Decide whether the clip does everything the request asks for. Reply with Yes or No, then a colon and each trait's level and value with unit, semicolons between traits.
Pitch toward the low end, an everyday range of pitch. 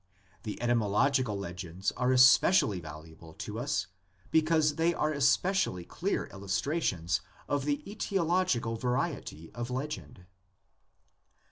No: low, 125 Hz; wide, 8.1 semitones